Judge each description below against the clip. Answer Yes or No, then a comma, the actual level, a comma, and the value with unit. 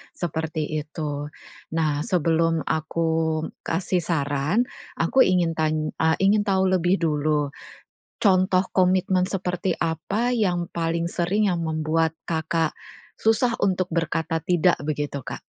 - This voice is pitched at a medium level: Yes, medium, 165 Hz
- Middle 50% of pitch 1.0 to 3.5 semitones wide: Yes, average, 2.8 semitones